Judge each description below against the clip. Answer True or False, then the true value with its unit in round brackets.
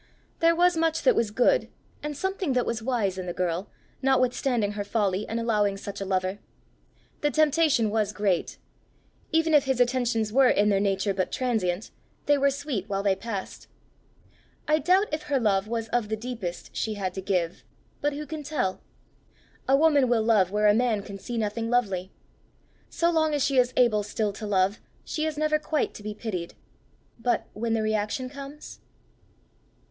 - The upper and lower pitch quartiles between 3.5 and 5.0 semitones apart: False (5.6 semitones)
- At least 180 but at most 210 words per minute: True (185 wpm)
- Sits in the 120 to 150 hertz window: False (230 Hz)